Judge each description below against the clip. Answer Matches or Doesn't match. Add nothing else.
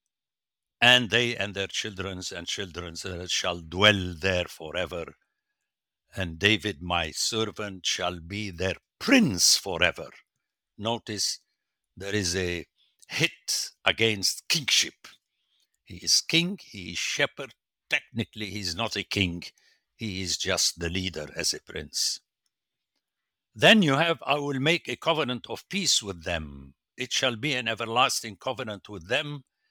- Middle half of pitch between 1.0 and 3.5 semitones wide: Doesn't match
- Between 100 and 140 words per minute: Matches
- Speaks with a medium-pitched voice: Doesn't match